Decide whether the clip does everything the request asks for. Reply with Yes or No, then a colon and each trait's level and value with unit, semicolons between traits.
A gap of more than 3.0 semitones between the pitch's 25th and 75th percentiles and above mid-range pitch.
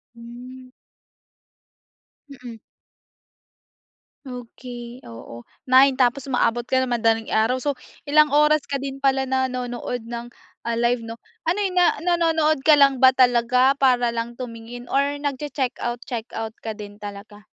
No: average, 2.7 semitones; very high, 250 Hz